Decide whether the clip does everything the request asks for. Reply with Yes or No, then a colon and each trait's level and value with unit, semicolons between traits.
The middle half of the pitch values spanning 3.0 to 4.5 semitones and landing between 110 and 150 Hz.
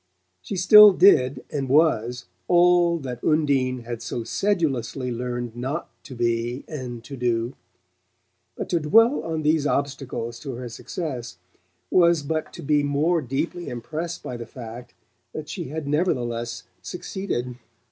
No: average, 5.1 semitones; medium, 140 Hz